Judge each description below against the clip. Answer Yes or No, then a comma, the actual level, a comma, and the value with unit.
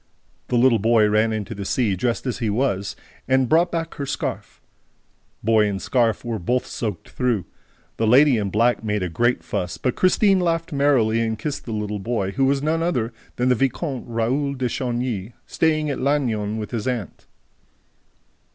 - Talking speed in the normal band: Yes, average, 185 wpm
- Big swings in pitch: No, average, 4.0 semitones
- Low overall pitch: Yes, low, 120 Hz